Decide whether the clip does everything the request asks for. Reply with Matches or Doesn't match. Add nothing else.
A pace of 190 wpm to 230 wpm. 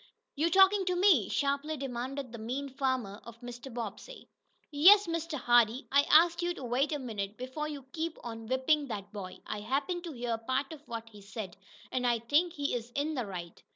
Matches